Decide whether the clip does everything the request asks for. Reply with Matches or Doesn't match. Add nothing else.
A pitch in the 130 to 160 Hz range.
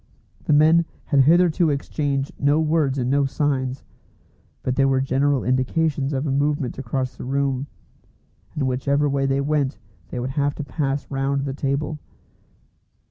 Matches